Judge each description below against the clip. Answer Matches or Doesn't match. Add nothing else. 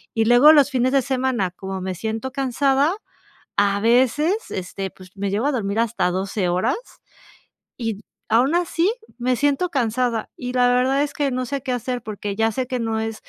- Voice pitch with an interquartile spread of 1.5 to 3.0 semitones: Doesn't match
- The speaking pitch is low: Doesn't match